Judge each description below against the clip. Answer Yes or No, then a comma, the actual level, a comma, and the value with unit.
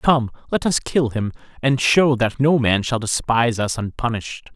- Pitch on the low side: Yes, low, 120 Hz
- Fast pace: No, average, 185 wpm